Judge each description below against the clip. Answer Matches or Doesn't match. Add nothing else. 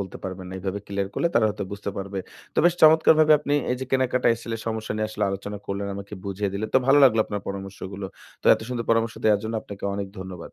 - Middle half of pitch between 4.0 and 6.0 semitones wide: Doesn't match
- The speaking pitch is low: Matches